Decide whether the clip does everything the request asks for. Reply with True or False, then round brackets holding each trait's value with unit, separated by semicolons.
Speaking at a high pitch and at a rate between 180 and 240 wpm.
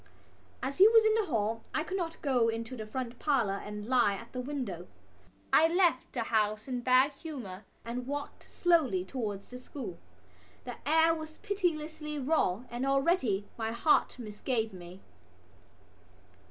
False (255 Hz; 155 wpm)